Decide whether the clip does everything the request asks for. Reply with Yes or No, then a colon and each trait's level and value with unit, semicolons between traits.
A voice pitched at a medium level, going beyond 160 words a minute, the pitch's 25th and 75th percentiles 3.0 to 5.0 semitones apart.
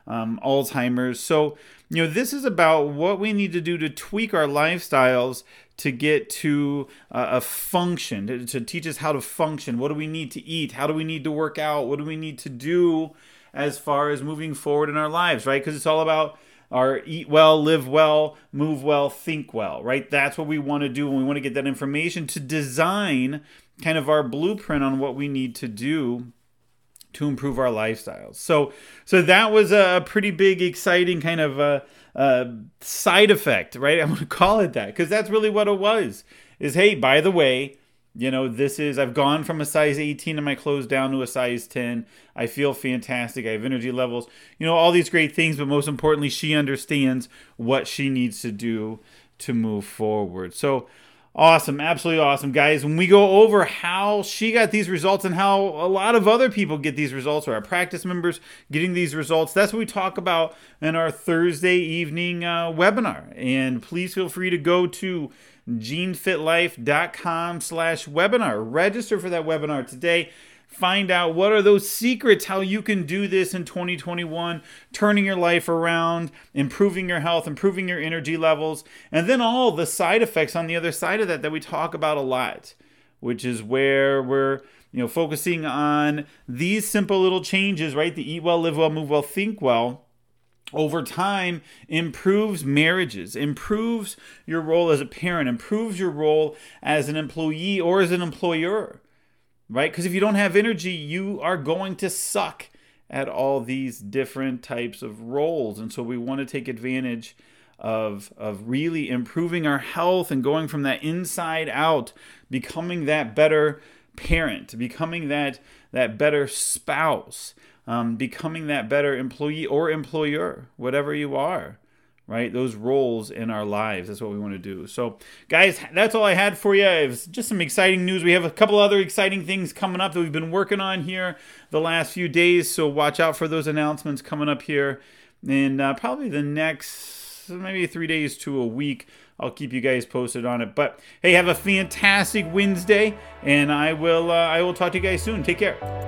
Yes: medium, 155 Hz; average, 190 wpm; average, 4.6 semitones